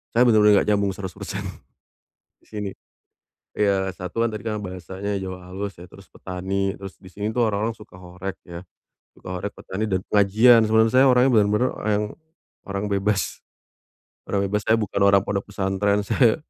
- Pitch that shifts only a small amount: Yes, narrow, 2.0 semitones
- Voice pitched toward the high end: No, low, 100 Hz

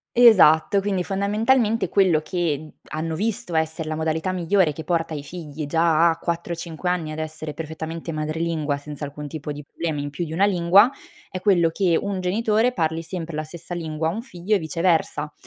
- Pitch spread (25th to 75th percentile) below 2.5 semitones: No, average, 2.9 semitones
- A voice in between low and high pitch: Yes, medium, 165 Hz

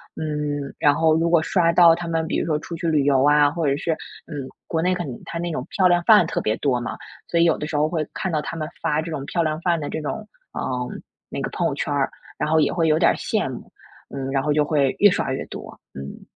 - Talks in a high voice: No, medium, 155 Hz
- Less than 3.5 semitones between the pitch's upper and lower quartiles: Yes, narrow, 2.6 semitones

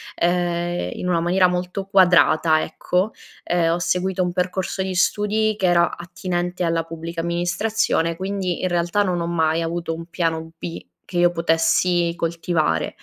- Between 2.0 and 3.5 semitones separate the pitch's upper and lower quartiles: No, narrow, 1.6 semitones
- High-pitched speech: No, medium, 175 Hz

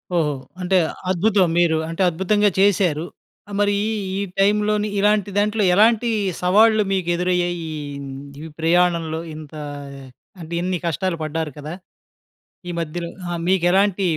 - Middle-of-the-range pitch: Yes, medium, 180 Hz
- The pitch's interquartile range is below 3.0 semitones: No, average, 3.5 semitones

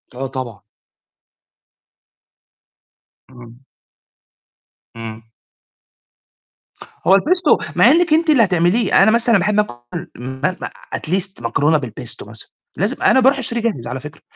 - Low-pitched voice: No, medium, 180 Hz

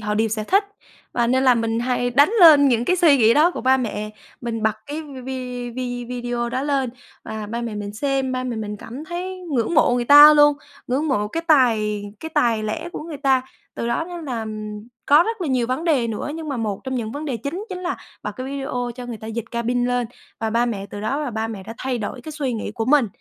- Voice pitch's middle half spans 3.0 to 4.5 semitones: Yes, average, 4.2 semitones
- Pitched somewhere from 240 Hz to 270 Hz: Yes, very high, 250 Hz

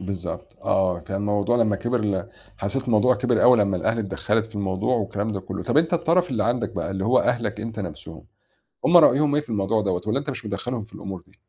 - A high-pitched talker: No, low, 110 Hz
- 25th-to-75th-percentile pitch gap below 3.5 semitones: No, average, 3.9 semitones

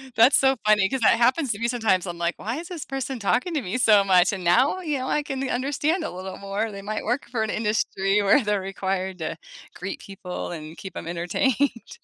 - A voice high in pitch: Yes, high, 215 Hz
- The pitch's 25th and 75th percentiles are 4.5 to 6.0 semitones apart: Yes, wide, 5.5 semitones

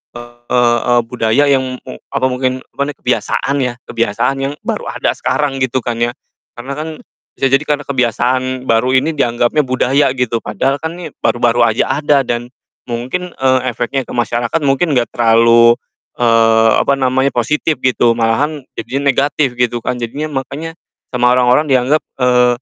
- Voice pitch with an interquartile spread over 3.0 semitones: No, narrow, 2.5 semitones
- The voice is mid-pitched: No, low, 125 Hz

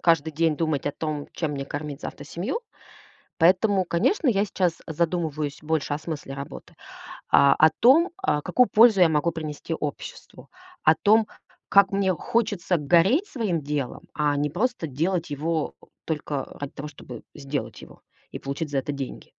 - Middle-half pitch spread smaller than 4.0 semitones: No, average, 4.3 semitones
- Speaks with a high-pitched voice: No, medium, 160 Hz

